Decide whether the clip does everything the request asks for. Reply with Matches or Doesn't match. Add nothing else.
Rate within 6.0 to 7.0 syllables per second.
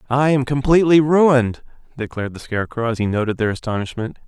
Matches